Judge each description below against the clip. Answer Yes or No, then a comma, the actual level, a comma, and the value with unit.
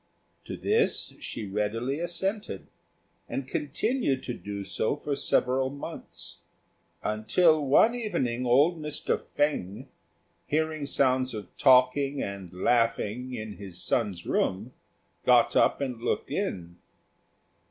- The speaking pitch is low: Yes, low, 130 Hz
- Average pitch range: No, wide, 5.7 semitones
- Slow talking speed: Yes, slow, 115 wpm